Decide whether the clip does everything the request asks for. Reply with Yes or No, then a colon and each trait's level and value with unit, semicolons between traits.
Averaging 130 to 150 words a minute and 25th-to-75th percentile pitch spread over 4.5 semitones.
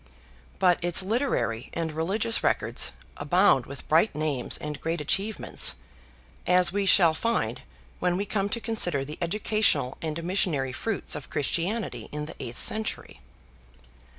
Yes: average, 140 wpm; average, 5.2 semitones